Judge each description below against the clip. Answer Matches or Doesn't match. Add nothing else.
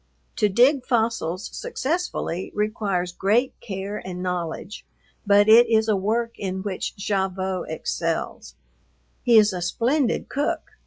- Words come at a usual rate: Doesn't match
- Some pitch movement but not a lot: Matches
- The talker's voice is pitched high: Matches